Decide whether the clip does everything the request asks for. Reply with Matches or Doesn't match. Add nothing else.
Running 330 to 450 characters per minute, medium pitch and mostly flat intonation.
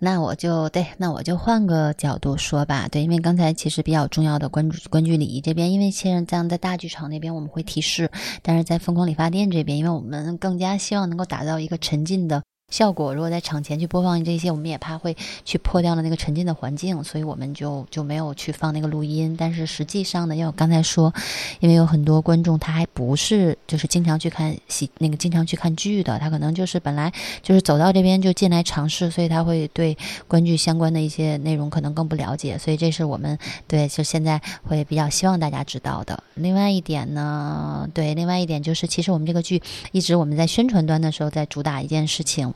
Matches